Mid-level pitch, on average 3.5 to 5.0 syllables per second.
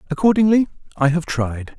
No: medium, 170 Hz; 5.4 syllables/s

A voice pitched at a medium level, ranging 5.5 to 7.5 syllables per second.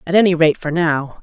Yes: medium, 165 Hz; 5.6 syllables/s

